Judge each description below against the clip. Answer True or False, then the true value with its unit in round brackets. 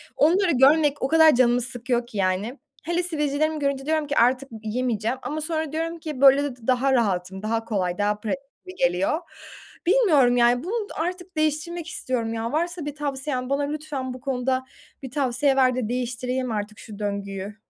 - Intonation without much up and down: False (4.7 semitones)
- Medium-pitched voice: False (265 Hz)